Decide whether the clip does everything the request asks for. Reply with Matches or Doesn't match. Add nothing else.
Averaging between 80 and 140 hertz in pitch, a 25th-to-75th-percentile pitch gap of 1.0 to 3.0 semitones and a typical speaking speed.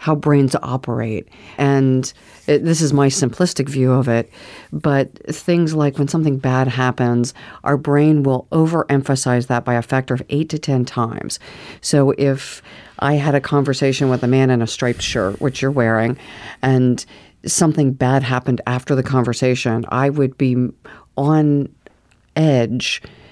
Matches